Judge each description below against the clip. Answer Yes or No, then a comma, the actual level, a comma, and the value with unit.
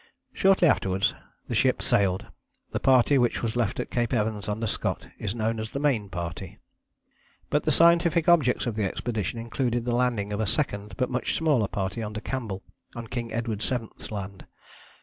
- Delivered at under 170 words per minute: No, average, 180 wpm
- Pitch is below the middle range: Yes, low, 115 Hz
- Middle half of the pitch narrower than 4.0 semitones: Yes, average, 3.4 semitones